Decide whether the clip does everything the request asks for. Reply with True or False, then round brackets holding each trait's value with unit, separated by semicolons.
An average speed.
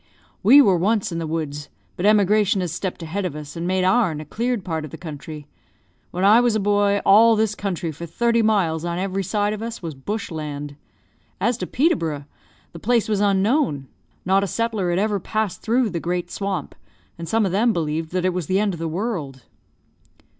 False (210 wpm)